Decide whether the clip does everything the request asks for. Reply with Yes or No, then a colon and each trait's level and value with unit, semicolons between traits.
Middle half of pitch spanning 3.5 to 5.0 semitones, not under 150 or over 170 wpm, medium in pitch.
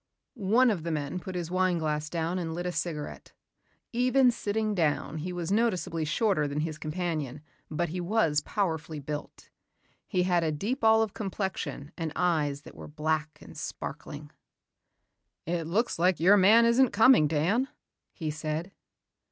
Yes: average, 4.6 semitones; average, 160 wpm; medium, 170 Hz